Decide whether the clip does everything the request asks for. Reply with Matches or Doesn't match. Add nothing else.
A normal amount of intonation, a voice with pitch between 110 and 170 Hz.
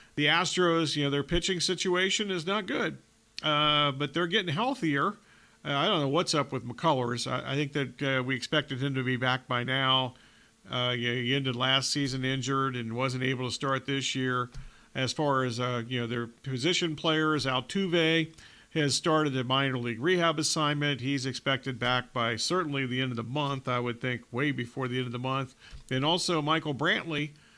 Matches